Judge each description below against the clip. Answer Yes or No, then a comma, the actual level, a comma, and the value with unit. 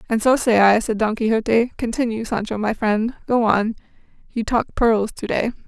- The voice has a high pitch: Yes, high, 225 Hz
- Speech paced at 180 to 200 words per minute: Yes, average, 190 wpm